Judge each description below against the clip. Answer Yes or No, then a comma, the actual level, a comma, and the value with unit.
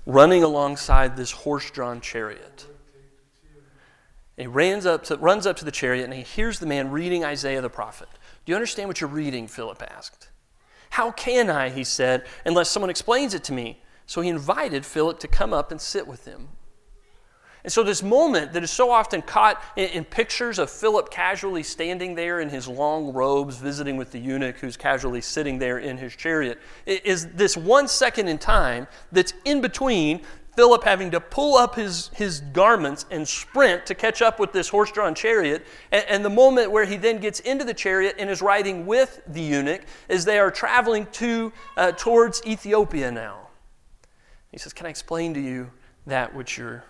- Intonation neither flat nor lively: No, wide, 7.5 semitones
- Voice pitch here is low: No, medium, 170 Hz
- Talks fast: No, average, 190 wpm